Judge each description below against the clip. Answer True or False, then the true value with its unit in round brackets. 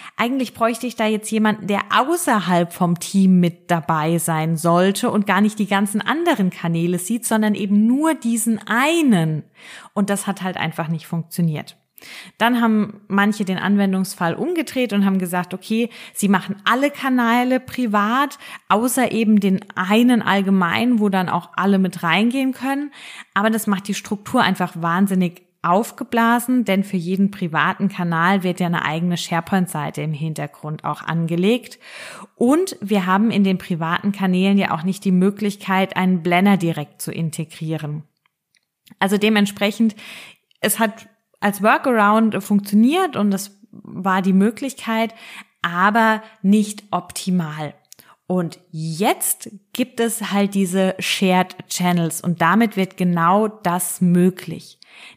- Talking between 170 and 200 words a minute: False (140 wpm)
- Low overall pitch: False (200 Hz)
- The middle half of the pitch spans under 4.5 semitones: True (4.0 semitones)